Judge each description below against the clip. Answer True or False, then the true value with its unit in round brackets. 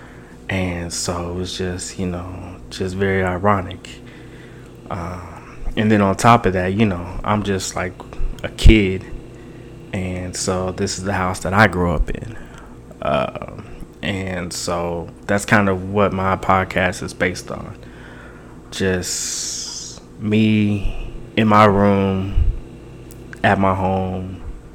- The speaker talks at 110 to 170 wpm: True (135 wpm)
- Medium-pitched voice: False (95 Hz)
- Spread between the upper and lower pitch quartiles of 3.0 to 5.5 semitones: False (2.5 semitones)